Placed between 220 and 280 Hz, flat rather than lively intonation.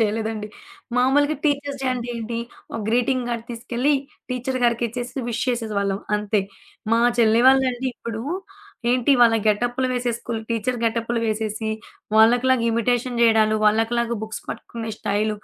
Yes: high, 235 Hz; narrow, 2.0 semitones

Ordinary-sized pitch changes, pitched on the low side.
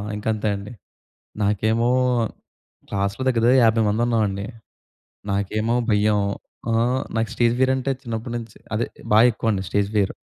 No: narrow, 2.3 semitones; low, 110 Hz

